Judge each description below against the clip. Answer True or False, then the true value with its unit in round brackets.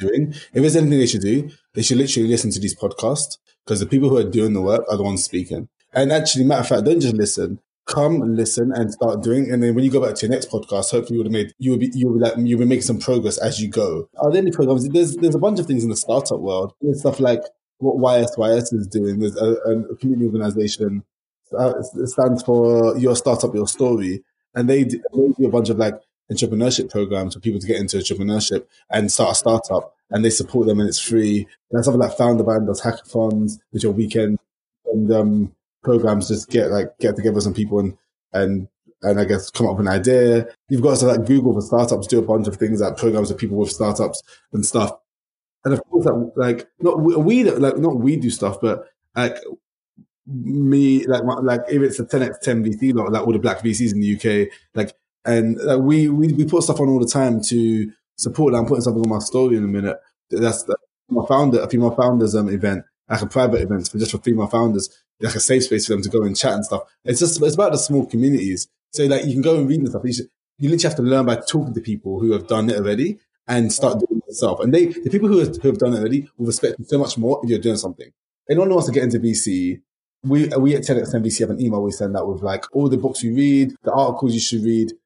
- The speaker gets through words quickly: True (245 wpm)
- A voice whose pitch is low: True (115 Hz)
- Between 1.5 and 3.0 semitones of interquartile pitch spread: False (3.7 semitones)